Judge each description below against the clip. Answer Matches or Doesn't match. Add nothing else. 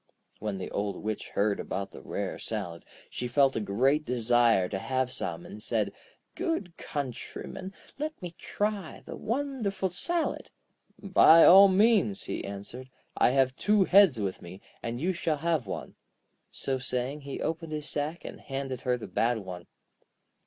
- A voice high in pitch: Doesn't match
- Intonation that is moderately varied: Doesn't match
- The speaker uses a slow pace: Doesn't match